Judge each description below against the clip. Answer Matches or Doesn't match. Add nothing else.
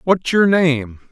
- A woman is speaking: Doesn't match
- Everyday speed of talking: Matches